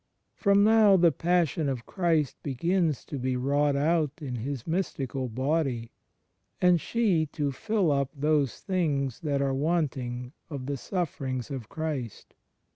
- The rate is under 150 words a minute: Yes, average, 140 wpm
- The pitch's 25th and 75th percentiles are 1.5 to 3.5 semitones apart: No, average, 4.3 semitones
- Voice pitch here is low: No, medium, 145 Hz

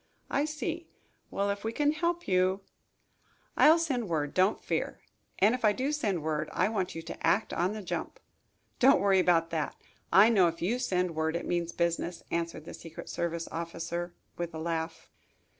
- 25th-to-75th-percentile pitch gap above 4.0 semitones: Yes, average, 5.1 semitones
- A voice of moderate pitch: Yes, medium, 180 Hz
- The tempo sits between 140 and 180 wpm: No, average, 190 wpm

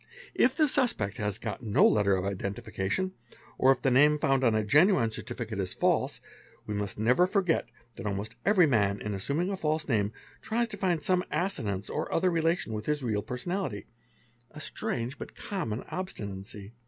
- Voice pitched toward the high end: No, low, 120 Hz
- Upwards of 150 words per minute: Yes, average, 180 wpm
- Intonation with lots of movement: Yes, wide, 8.4 semitones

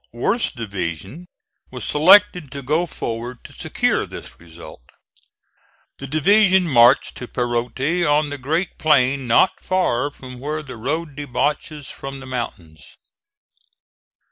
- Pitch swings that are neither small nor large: Yes, average, 4.5 semitones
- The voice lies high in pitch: No, low, 135 Hz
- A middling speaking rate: No, slow, 125 wpm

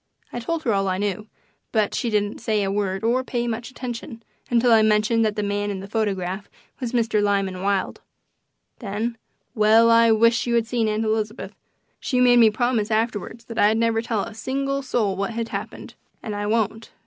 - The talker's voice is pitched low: No, high, 220 Hz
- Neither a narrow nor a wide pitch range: No, narrow, 2.2 semitones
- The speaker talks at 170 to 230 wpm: Yes, average, 195 wpm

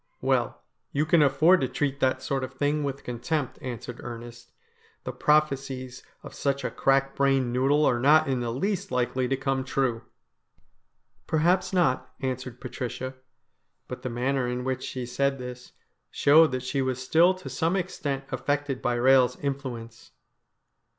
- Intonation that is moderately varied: No, narrow, 2.3 semitones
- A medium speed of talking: Yes, average, 165 wpm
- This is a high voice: No, low, 135 Hz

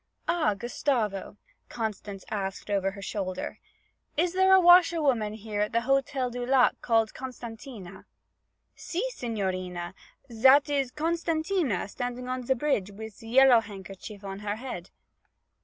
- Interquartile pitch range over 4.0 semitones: Yes, average, 5.0 semitones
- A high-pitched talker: Yes, high, 230 Hz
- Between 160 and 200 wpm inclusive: No, average, 140 wpm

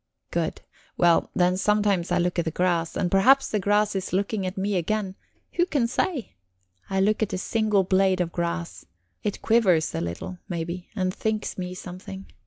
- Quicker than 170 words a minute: Yes, average, 185 wpm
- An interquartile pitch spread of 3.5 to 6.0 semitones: No, average, 2.8 semitones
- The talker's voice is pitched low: No, high, 190 Hz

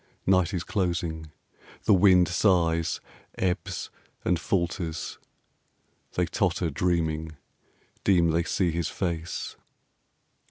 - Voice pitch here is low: Yes, very low, 85 Hz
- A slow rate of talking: Yes, slow, 95 wpm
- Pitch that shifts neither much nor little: No, narrow, 2.0 semitones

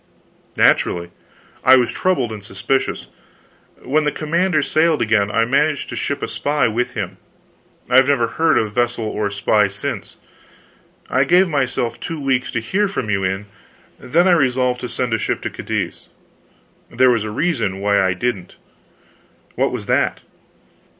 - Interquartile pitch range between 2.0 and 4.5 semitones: No, wide, 5.6 semitones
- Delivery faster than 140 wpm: Yes, average, 165 wpm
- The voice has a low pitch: Yes, low, 125 Hz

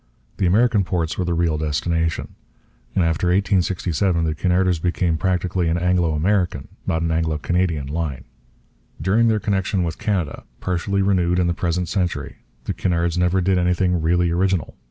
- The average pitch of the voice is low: Yes, very low, 90 Hz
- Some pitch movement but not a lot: No, narrow, 2.1 semitones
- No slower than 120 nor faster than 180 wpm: Yes, average, 160 wpm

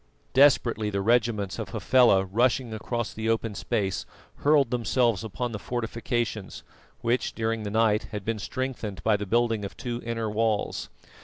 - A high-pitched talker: No, low, 115 Hz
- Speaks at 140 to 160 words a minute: Yes, average, 155 wpm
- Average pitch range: No, narrow, 2.3 semitones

